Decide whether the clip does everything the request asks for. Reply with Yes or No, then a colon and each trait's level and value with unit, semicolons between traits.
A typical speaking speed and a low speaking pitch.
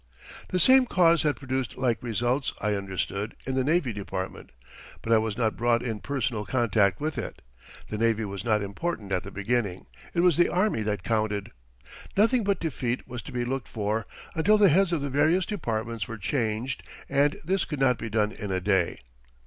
Yes: average, 195 wpm; low, 120 Hz